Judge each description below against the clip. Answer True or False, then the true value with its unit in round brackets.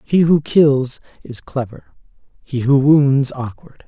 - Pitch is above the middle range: False (140 Hz)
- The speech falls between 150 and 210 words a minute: False (140 wpm)